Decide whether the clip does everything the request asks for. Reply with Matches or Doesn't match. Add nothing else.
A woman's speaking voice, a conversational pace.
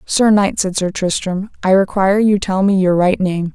Doesn't match